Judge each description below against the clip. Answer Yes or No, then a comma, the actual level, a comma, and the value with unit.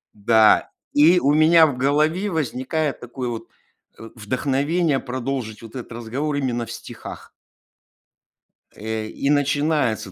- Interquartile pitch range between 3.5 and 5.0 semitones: Yes, average, 4.6 semitones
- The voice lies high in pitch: No, low, 135 Hz